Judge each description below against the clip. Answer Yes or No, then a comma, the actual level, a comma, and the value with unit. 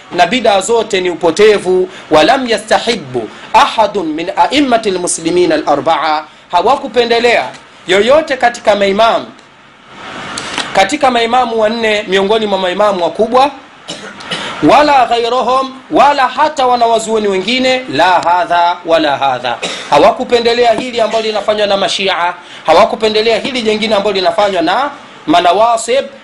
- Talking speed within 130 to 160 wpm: No, average, 105 wpm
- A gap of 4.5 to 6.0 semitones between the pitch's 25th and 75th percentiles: Yes, average, 4.8 semitones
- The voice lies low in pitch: No, high, 225 Hz